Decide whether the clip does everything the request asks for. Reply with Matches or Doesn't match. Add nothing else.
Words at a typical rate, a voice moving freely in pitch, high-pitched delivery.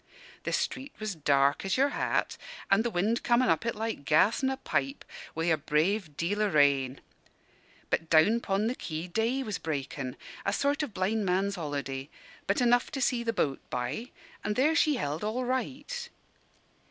Matches